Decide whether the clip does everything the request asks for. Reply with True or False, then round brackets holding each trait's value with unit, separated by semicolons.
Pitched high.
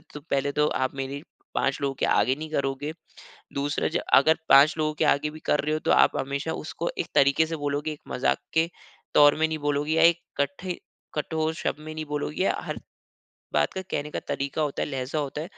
False (145 Hz)